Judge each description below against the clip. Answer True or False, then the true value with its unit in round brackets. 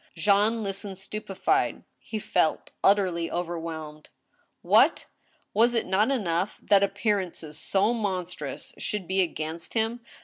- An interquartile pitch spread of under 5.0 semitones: True (3.8 semitones)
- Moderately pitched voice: False (195 Hz)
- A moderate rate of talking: False (115 wpm)